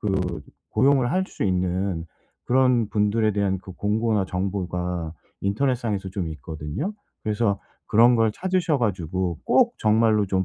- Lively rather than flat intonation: No, average, 3.9 semitones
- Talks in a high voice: No, low, 100 Hz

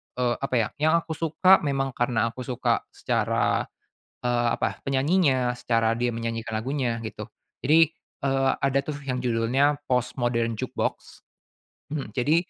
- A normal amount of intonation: Yes, average, 3.3 semitones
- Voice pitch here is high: No, low, 130 Hz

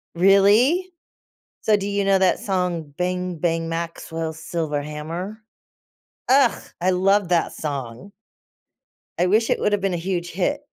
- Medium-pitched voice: Yes, medium, 180 Hz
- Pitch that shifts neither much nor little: Yes, average, 3.4 semitones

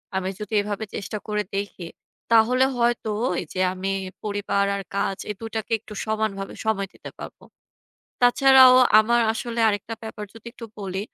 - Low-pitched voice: No, high, 215 Hz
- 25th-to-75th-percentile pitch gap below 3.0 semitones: Yes, narrow, 2.6 semitones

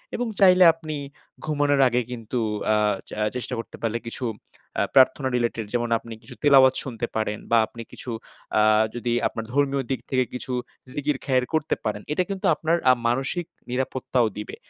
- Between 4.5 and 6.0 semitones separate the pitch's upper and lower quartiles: No, average, 3.6 semitones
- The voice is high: No, low, 130 Hz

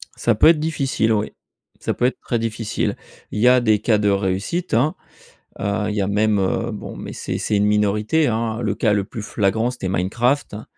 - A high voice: No, low, 110 Hz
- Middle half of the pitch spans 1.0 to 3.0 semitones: Yes, average, 2.7 semitones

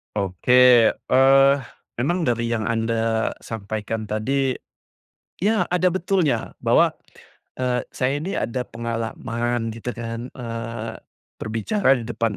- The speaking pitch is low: Yes, low, 120 Hz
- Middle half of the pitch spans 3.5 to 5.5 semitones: No, average, 2.9 semitones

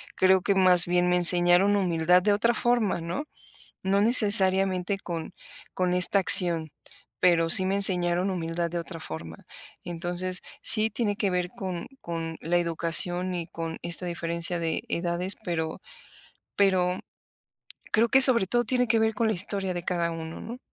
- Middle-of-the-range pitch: Yes, medium, 180 Hz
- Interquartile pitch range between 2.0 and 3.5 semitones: Yes, average, 2.7 semitones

